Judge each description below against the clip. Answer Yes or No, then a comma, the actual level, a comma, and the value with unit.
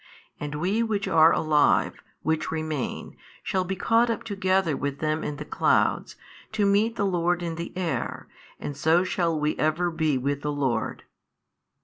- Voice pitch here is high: No, medium, 165 Hz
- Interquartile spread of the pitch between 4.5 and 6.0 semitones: No, average, 4.1 semitones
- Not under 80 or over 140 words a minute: No, average, 165 wpm